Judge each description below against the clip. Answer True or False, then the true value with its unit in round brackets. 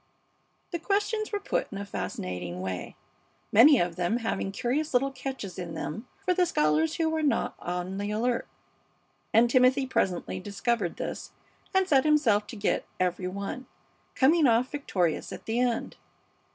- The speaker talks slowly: False (160 wpm)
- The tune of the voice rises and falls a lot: True (7.4 semitones)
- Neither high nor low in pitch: False (235 Hz)